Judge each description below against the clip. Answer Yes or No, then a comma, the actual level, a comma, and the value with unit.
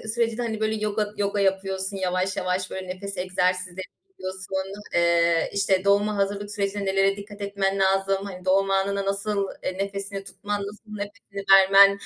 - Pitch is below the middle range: No, high, 195 Hz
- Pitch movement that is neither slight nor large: No, narrow, 1.1 semitones